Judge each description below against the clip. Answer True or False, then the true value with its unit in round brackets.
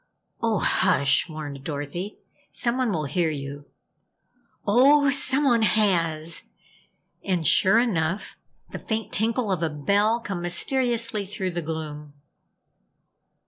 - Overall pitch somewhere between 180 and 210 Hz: True (190 Hz)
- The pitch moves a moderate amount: False (6.6 semitones)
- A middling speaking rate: False (110 wpm)